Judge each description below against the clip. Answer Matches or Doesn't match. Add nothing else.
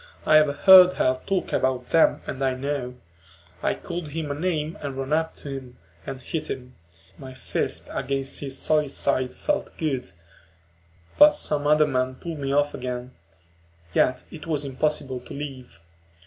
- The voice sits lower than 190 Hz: Matches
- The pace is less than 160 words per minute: Doesn't match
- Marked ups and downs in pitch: Doesn't match